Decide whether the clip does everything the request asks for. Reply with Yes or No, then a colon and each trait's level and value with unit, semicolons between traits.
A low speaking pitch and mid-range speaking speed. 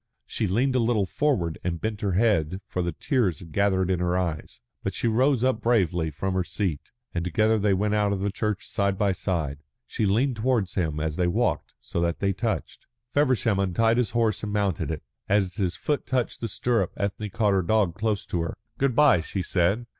No: low, 100 Hz; fast, 215 wpm